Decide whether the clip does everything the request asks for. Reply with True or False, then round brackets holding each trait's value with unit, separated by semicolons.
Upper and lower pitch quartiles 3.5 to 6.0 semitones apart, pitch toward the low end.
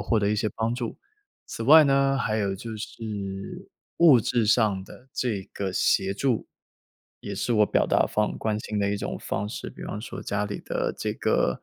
False (2.8 semitones; 105 Hz)